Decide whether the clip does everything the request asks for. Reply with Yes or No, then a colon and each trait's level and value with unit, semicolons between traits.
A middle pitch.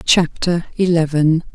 Yes: medium, 165 Hz